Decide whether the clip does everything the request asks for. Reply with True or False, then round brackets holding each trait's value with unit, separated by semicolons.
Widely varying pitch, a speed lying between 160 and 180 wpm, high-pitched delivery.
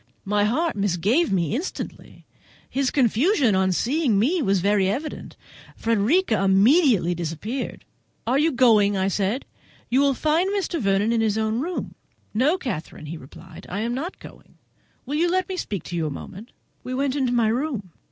True (6.5 semitones; 170 wpm; 230 Hz)